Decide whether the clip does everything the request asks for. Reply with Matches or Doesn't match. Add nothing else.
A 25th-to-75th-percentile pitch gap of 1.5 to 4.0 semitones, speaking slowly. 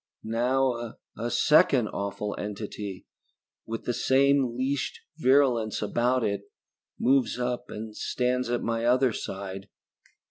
Matches